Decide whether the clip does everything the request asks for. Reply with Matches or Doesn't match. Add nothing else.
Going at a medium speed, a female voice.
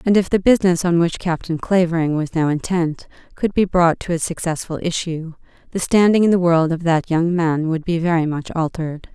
Doesn't match